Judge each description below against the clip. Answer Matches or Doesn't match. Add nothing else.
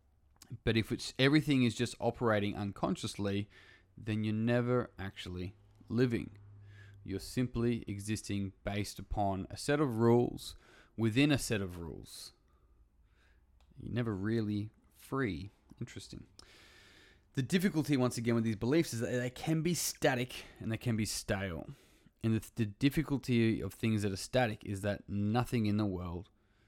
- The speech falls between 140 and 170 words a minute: Matches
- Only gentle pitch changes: Doesn't match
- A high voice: Doesn't match